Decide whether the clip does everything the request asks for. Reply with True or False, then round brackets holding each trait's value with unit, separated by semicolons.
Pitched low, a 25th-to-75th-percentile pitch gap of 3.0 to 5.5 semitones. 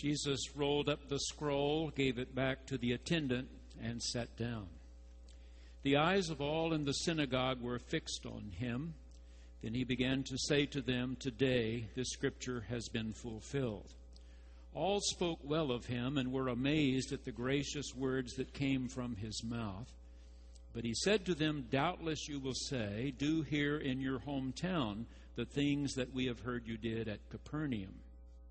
True (130 Hz; 3.8 semitones)